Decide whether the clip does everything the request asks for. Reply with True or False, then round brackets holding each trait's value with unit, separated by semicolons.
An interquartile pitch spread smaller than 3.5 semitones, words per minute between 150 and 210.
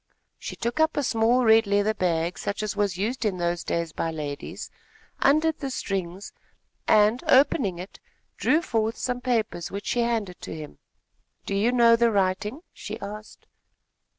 False (4.4 semitones; 165 wpm)